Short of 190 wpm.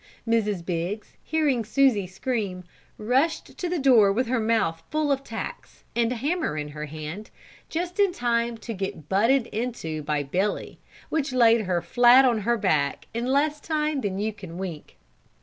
Yes: average, 170 wpm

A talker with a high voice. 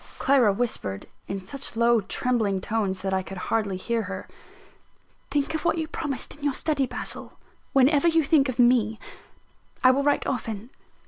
Yes: high, 240 Hz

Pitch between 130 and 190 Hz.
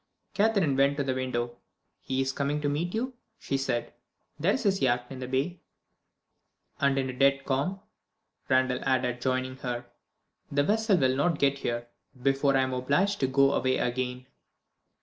Yes: low, 135 Hz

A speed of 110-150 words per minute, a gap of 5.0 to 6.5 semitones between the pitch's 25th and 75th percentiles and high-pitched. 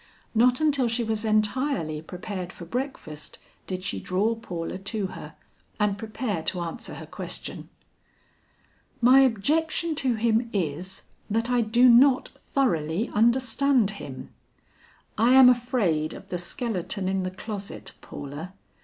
Yes: slow, 135 wpm; average, 5.3 semitones; high, 215 Hz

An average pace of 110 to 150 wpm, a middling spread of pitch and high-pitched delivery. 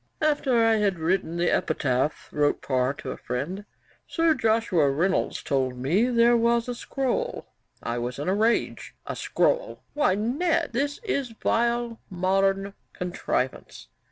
No: average, 145 wpm; wide, 7.2 semitones; high, 200 Hz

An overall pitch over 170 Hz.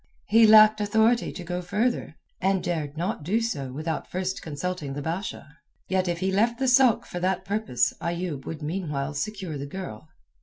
Yes: medium, 185 Hz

